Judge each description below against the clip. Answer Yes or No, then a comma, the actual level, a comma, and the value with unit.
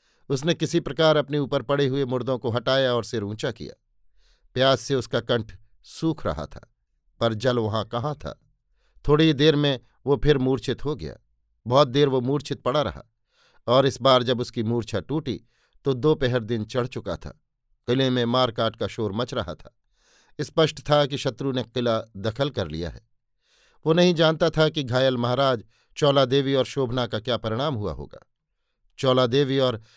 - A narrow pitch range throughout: No, average, 3.5 semitones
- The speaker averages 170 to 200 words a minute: Yes, average, 180 wpm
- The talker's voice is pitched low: Yes, low, 130 Hz